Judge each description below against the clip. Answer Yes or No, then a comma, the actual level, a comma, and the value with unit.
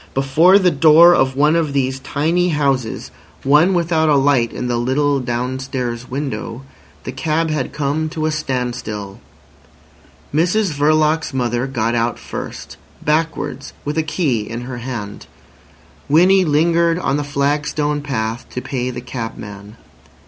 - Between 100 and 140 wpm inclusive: Yes, slow, 135 wpm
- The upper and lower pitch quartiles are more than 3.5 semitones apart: Yes, average, 4.1 semitones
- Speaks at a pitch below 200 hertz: Yes, medium, 140 Hz